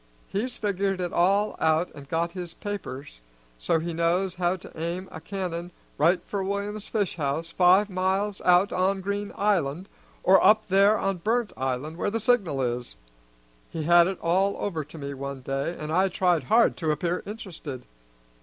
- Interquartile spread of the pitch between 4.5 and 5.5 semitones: No, average, 3.7 semitones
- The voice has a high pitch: No, medium, 180 Hz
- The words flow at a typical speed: Yes, average, 175 wpm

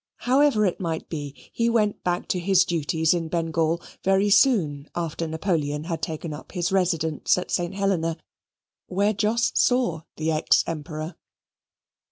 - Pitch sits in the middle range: Yes, medium, 170 Hz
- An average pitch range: Yes, average, 3.5 semitones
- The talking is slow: No, average, 150 wpm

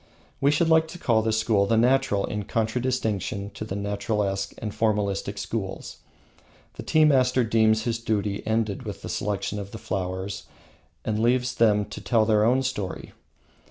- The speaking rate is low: No, average, 165 wpm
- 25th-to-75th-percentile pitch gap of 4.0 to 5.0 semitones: No, average, 3.2 semitones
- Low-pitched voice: Yes, low, 110 Hz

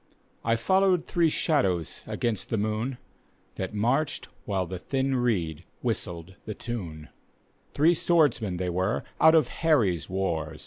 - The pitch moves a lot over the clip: Yes, wide, 7.2 semitones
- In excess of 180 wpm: No, slow, 135 wpm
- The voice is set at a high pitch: No, low, 110 Hz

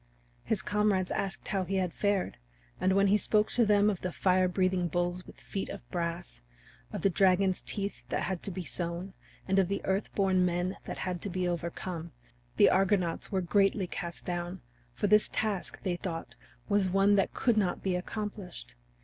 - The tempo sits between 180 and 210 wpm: Yes, average, 190 wpm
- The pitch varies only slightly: Yes, narrow, 2.0 semitones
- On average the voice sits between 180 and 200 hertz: Yes, medium, 185 Hz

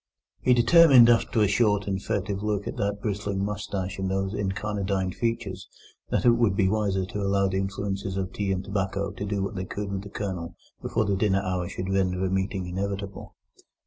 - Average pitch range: No, narrow, 1.4 semitones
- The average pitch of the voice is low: Yes, low, 100 Hz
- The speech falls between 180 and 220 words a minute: Yes, average, 200 wpm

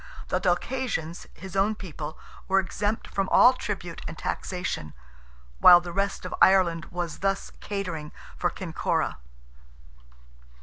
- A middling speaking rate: No, slow, 120 wpm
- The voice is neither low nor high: Yes, medium, 180 Hz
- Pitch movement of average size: Yes, average, 3.6 semitones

